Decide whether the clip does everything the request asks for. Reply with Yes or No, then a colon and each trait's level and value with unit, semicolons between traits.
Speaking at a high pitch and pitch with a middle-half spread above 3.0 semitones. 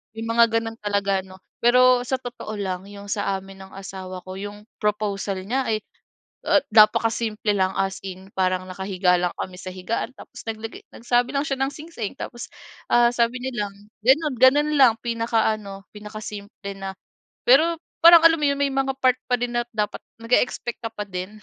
Yes: high, 220 Hz; average, 4.1 semitones